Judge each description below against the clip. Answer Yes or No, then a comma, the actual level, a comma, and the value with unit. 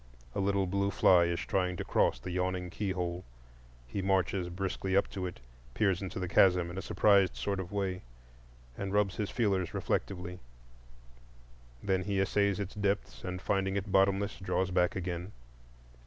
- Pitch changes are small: Yes, narrow, 1.5 semitones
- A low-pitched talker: Yes, very low, 95 Hz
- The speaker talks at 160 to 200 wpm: Yes, average, 165 wpm